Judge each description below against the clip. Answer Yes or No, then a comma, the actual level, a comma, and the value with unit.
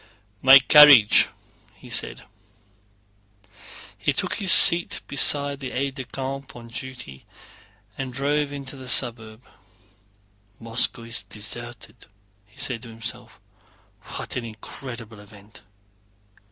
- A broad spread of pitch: No, average, 3.2 semitones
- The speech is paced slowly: Yes, slow, 110 wpm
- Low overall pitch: Yes, low, 125 Hz